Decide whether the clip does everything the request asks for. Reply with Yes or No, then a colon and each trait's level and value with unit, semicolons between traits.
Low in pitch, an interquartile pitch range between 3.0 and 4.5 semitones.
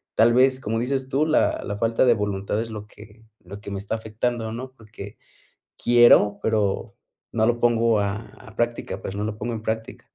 No: low, 110 Hz; narrow, 2.4 semitones